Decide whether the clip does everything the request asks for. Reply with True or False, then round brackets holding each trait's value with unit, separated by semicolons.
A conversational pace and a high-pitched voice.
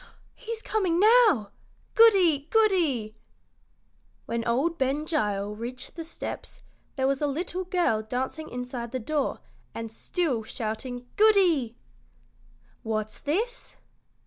False (115 wpm; 275 Hz)